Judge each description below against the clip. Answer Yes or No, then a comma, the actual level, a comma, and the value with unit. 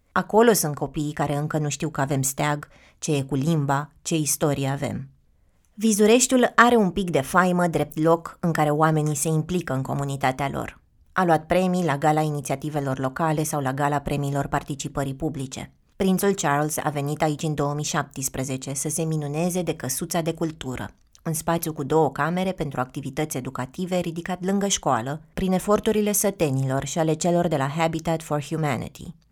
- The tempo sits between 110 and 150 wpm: No, fast, 170 wpm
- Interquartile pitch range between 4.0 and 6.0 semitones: No, average, 3.3 semitones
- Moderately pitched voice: Yes, medium, 155 Hz